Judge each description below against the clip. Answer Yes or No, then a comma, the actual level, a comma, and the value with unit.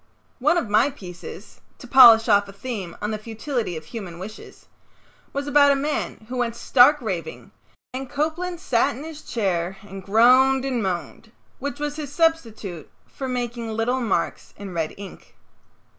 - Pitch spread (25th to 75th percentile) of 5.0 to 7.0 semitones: Yes, wide, 5.5 semitones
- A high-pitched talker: Yes, high, 235 Hz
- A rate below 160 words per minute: No, average, 165 wpm